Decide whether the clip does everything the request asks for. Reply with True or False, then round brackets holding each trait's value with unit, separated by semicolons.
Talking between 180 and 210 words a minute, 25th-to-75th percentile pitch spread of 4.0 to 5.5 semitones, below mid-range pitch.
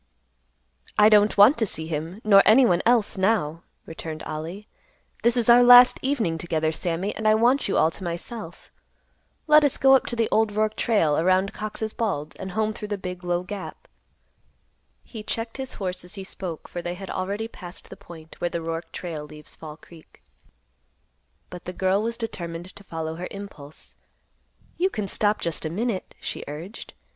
False (185 wpm; 4.6 semitones; 190 Hz)